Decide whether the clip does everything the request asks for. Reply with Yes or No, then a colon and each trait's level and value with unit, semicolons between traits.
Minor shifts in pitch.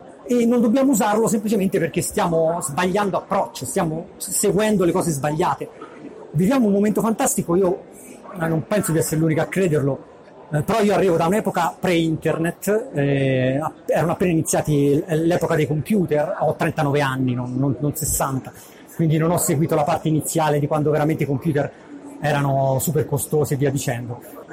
No: average, 4.5 semitones